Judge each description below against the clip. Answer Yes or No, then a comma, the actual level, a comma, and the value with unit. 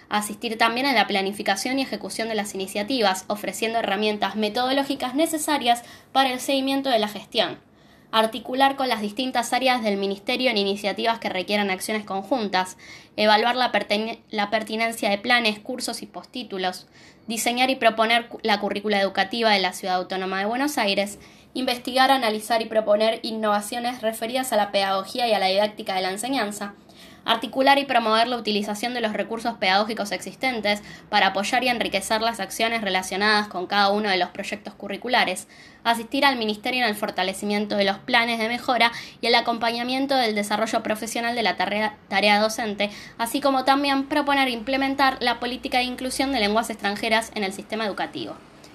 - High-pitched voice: Yes, high, 220 Hz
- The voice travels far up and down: No, average, 3.3 semitones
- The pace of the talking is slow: No, average, 165 wpm